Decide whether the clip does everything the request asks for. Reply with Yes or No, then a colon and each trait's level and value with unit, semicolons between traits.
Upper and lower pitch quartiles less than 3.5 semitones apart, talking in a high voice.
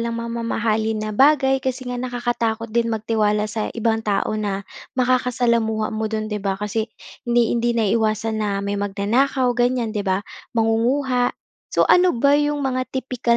Yes: narrow, 2.5 semitones; high, 230 Hz